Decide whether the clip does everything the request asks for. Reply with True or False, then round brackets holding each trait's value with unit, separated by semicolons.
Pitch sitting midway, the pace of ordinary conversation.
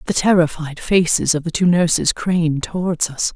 True (165 Hz; 180 wpm)